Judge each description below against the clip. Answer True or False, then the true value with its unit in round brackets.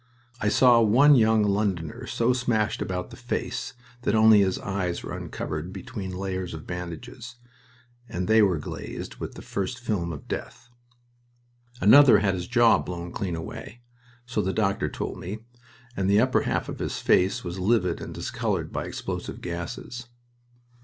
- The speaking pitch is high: False (100 Hz)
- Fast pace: False (160 wpm)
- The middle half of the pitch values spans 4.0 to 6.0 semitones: True (4.4 semitones)